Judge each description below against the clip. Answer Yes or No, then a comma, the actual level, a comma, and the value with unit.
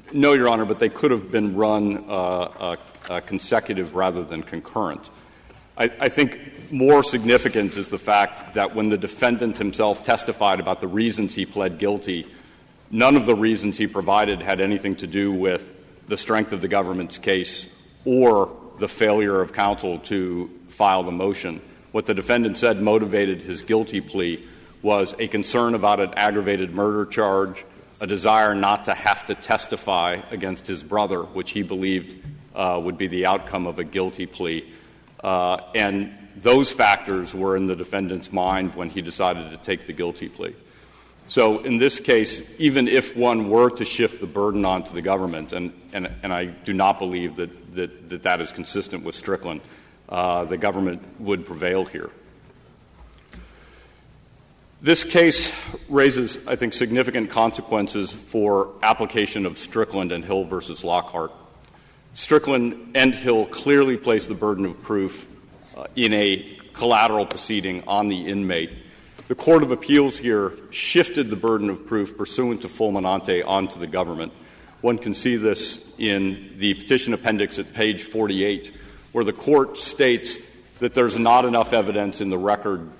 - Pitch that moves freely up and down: No, average, 3.2 semitones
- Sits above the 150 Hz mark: No, low, 100 Hz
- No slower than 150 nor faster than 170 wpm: Yes, average, 160 wpm